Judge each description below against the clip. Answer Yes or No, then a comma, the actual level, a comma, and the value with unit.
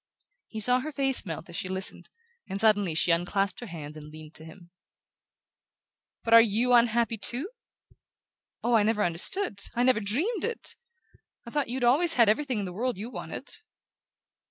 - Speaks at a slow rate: No, average, 175 wpm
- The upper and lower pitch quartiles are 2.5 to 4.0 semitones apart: No, average, 5.0 semitones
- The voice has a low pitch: No, high, 220 Hz